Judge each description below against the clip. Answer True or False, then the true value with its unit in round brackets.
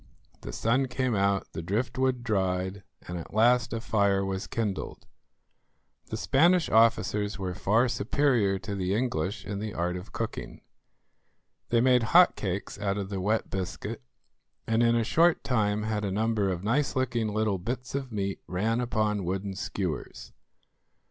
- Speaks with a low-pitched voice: True (105 Hz)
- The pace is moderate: True (160 wpm)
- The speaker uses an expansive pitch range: False (3.5 semitones)